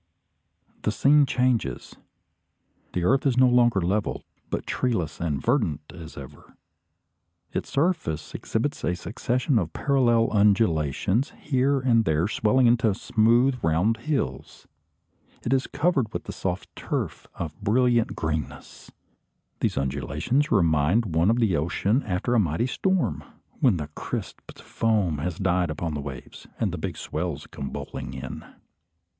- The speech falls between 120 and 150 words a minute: Yes, average, 140 wpm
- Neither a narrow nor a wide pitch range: No, wide, 7.7 semitones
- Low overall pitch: Yes, low, 105 Hz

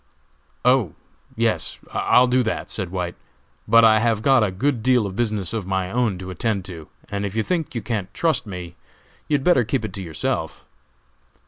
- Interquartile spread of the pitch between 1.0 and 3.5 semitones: No, average, 4.7 semitones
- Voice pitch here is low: Yes, low, 110 Hz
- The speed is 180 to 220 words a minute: Yes, average, 195 wpm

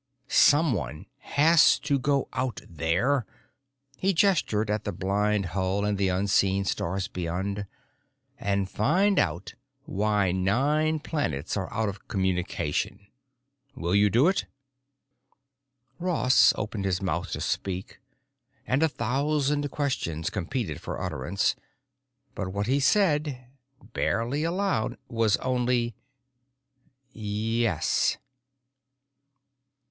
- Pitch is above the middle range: No, low, 110 Hz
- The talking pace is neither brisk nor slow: No, slow, 105 wpm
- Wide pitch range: Yes, wide, 6.7 semitones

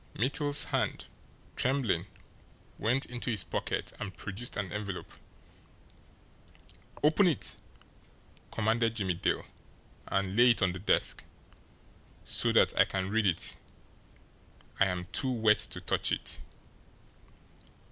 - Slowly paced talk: Yes, slow, 115 wpm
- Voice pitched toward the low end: Yes, low, 110 Hz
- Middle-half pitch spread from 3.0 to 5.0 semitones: Yes, average, 4.2 semitones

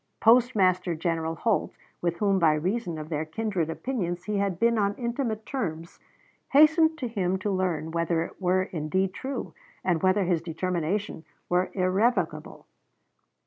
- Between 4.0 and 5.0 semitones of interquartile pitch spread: Yes, average, 4.5 semitones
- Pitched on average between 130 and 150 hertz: No, medium, 185 Hz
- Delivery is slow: No, average, 145 wpm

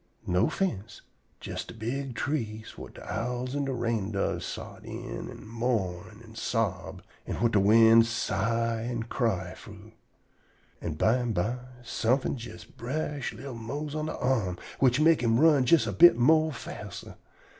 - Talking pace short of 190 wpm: Yes, average, 155 wpm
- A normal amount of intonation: Yes, average, 3.3 semitones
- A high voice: No, low, 115 Hz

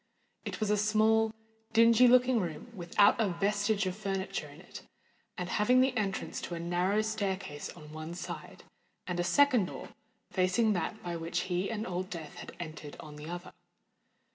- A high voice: Yes, high, 195 Hz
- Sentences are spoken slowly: No, average, 175 wpm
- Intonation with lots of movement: No, average, 3.8 semitones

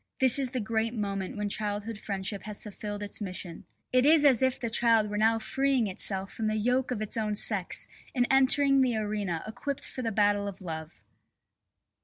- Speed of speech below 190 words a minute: No, average, 195 wpm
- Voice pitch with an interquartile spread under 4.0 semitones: Yes, average, 3.5 semitones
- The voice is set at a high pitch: Yes, high, 215 Hz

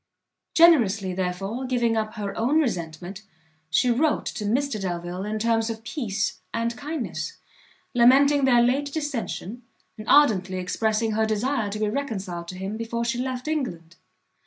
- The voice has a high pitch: Yes, high, 225 Hz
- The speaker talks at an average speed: Yes, average, 150 wpm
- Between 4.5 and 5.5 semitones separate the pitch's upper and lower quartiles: Yes, average, 4.8 semitones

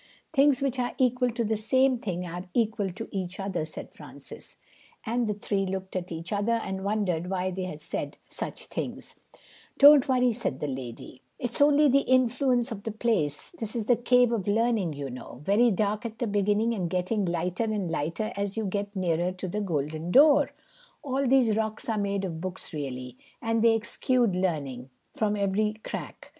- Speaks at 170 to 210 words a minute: Yes, average, 190 wpm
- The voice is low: No, high, 205 Hz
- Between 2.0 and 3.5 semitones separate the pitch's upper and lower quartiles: No, average, 4.6 semitones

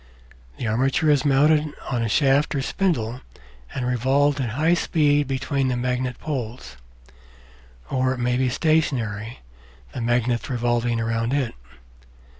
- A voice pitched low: Yes, low, 130 Hz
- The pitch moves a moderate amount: Yes, average, 3.1 semitones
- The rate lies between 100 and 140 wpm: Yes, slow, 135 wpm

